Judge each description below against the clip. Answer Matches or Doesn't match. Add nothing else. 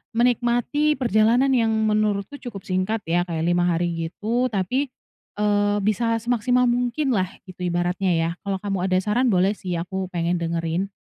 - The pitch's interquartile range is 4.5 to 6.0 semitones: Matches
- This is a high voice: Matches